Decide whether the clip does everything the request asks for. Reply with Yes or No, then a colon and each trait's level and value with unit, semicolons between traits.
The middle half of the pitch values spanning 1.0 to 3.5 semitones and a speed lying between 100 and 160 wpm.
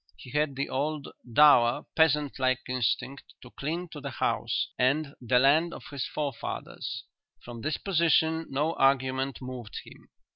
Yes: average, 3.1 semitones; average, 150 wpm